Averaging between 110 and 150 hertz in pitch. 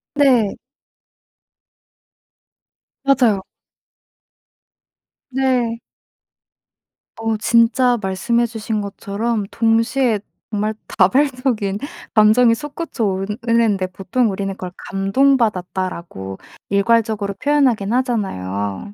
No: high, 220 Hz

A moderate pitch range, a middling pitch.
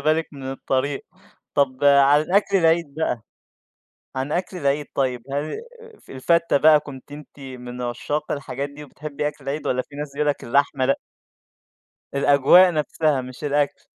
No: narrow, 2.1 semitones; medium, 145 Hz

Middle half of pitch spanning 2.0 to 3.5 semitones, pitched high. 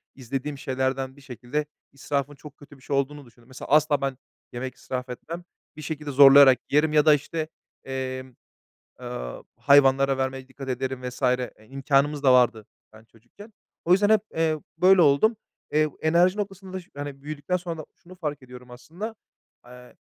No: average, 2.9 semitones; medium, 140 Hz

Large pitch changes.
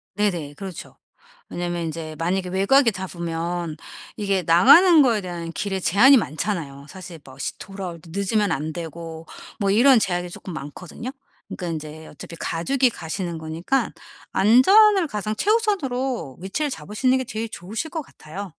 Yes: wide, 5.7 semitones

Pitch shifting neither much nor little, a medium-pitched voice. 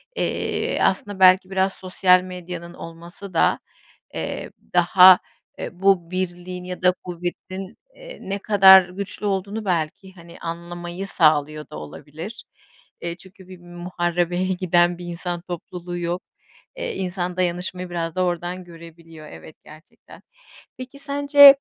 No: narrow, 1.7 semitones; medium, 180 Hz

